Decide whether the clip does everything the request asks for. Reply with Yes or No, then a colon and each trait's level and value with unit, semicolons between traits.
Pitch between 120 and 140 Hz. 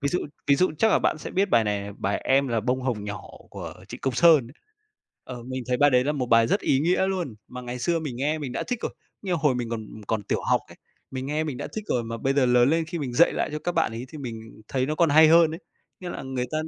Yes: low, 135 Hz